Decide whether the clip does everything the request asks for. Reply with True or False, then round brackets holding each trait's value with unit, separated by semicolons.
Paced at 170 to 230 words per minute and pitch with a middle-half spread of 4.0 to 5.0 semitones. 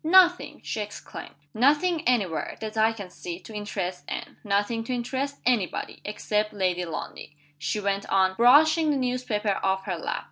True (175 wpm; 4.6 semitones)